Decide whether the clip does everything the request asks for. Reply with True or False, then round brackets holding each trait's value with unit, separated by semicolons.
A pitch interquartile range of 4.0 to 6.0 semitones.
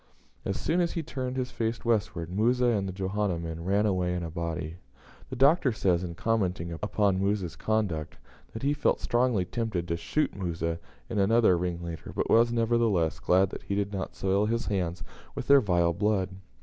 True (4.7 semitones)